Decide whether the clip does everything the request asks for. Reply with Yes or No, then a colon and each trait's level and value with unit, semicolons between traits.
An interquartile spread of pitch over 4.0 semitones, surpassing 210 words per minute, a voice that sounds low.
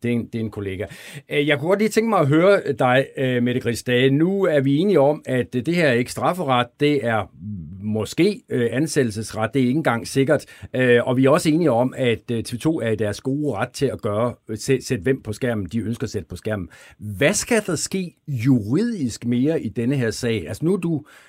Yes: average, 4.6 semitones; fast, 225 wpm; low, 125 Hz